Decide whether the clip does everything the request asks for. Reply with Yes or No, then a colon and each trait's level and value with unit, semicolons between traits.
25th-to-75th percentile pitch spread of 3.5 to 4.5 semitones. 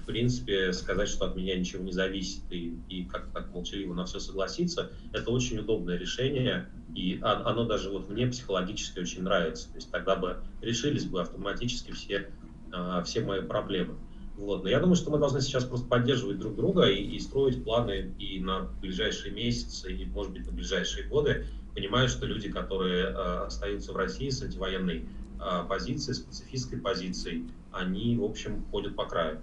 No: average, 5.0 semitones